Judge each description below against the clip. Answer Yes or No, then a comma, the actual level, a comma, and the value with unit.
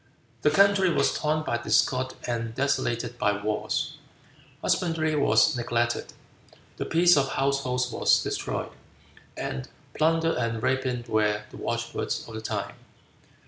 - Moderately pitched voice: No, low, 130 Hz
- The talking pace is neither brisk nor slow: No, slow, 130 wpm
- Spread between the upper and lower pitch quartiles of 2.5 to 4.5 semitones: No, average, 4.9 semitones